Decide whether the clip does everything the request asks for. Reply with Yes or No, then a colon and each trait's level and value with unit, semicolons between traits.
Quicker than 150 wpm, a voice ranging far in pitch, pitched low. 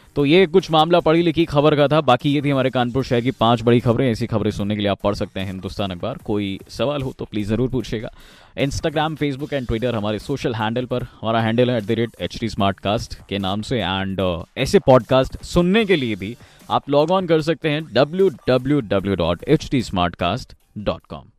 Yes: average, 185 wpm; wide, 5.7 semitones; low, 125 Hz